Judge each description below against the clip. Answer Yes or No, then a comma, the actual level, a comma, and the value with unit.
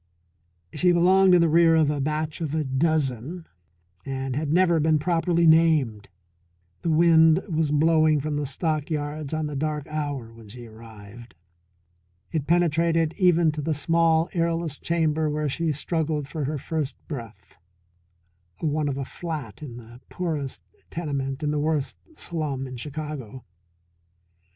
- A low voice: No, medium, 155 Hz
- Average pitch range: Yes, average, 3.1 semitones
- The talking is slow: No, average, 145 wpm